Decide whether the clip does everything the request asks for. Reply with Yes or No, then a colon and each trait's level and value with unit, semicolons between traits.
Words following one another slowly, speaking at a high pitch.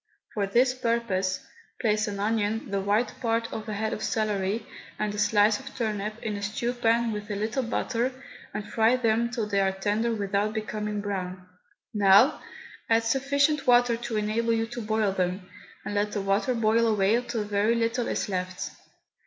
No: average, 180 wpm; high, 215 Hz